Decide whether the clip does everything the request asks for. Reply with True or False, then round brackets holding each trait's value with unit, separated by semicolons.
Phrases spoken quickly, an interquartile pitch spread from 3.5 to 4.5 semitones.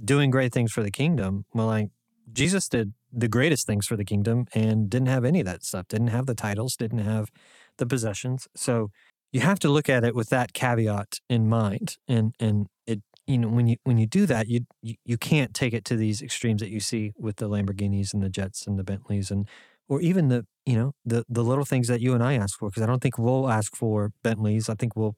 False (245 wpm; 2.9 semitones)